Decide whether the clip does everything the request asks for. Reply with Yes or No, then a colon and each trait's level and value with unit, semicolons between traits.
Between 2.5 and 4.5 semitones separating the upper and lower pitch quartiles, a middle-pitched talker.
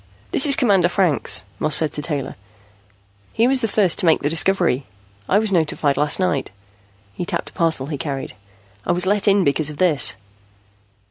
No: average, 4.9 semitones; medium, 170 Hz